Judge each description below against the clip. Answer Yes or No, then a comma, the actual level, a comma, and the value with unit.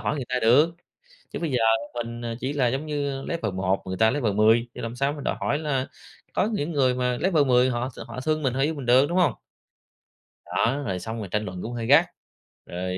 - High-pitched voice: No, low, 125 Hz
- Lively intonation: No, average, 4.1 semitones